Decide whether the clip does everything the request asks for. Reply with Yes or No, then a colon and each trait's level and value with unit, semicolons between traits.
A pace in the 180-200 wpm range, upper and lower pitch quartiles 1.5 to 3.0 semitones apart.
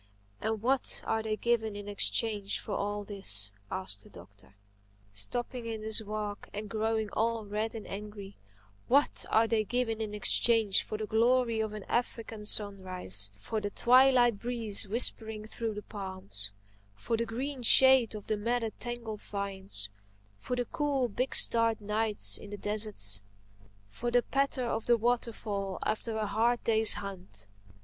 No: average, 155 wpm; narrow, 2.5 semitones